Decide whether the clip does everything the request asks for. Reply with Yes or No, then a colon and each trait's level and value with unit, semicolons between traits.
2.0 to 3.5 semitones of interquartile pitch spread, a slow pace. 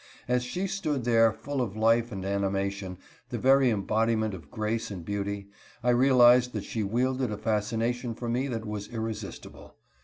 No: average, 3.2 semitones; average, 165 wpm